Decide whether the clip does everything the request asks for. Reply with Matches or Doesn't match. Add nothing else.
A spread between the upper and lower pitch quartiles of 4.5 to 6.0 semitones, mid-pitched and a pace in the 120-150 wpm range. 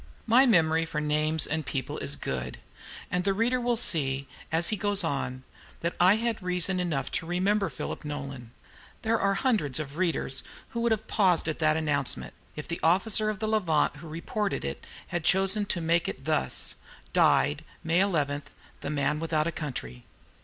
Doesn't match